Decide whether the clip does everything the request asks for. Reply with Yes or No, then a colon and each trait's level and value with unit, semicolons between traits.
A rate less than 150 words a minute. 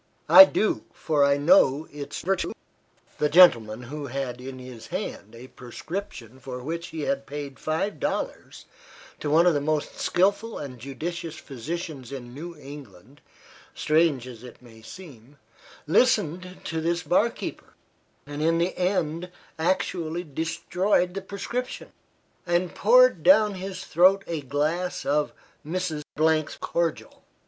Yes: average, 140 wpm